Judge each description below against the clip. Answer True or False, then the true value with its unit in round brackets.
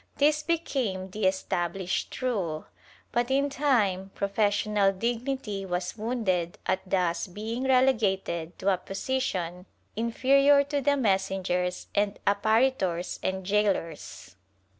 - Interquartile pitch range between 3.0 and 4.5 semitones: False (5.4 semitones)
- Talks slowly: True (115 wpm)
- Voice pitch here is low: False (200 Hz)